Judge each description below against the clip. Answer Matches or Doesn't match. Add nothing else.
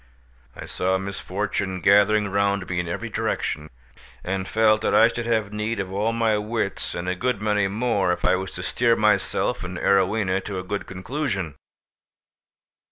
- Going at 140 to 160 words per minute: Doesn't match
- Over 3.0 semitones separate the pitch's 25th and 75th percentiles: Doesn't match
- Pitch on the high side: Doesn't match